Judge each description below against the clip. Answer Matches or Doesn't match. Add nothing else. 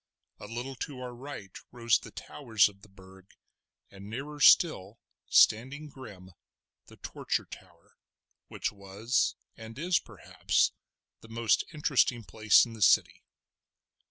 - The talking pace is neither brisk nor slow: Doesn't match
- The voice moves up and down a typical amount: Matches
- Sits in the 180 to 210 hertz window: Doesn't match